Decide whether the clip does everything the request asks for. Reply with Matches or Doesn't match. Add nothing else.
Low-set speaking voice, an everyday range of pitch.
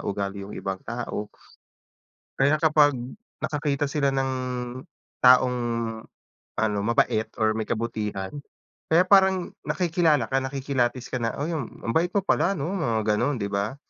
Doesn't match